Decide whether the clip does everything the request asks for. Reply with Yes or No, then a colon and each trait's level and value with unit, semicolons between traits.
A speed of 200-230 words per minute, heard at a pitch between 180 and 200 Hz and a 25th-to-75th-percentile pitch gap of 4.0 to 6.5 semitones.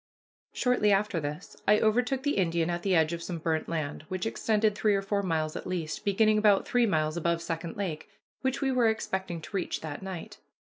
Yes: fast, 205 wpm; high, 190 Hz; average, 4.4 semitones